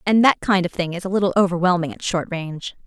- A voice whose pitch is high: No, medium, 180 Hz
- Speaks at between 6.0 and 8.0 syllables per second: Yes, 6.5 syllables/s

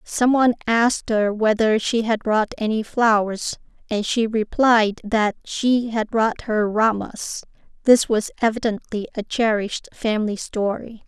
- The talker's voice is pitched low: No, high, 220 Hz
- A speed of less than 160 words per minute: Yes, average, 140 wpm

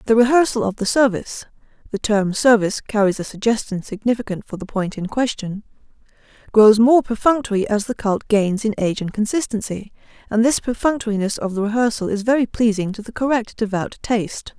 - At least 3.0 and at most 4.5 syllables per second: Yes, 4.4 syllables/s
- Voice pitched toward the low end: No, high, 220 Hz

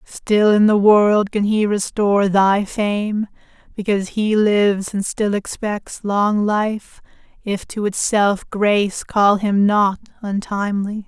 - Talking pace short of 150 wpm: Yes, slow, 135 wpm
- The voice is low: No, high, 205 Hz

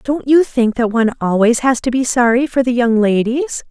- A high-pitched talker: Yes, high, 245 Hz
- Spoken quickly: Yes, fast, 225 wpm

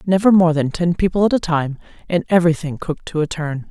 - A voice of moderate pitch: Yes, medium, 165 Hz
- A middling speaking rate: No, fast, 225 wpm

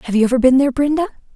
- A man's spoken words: No, female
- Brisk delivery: Yes, fast, 265 wpm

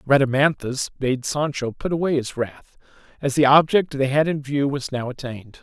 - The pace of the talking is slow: No, average, 180 wpm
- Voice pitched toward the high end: No, medium, 140 Hz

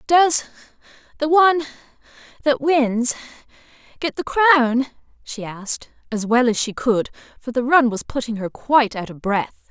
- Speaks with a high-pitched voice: Yes, very high, 260 Hz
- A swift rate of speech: No, slow, 135 wpm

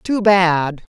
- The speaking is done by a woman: Yes, female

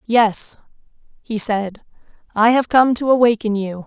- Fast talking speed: No, average, 140 wpm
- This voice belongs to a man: No, female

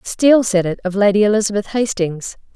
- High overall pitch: Yes, high, 205 Hz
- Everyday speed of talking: Yes, average, 165 wpm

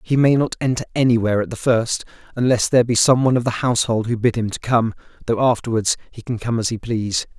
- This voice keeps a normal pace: No, fast, 235 wpm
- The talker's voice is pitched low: Yes, low, 115 Hz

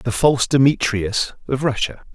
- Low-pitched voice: Yes, low, 120 Hz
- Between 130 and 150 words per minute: Yes, average, 140 wpm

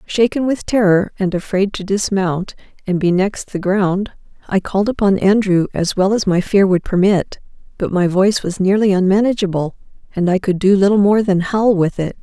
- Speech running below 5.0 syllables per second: No, 5.1 syllables/s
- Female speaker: Yes, female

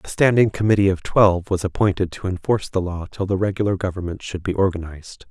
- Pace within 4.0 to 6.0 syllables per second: No, 6.4 syllables/s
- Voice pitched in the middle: No, very low, 95 Hz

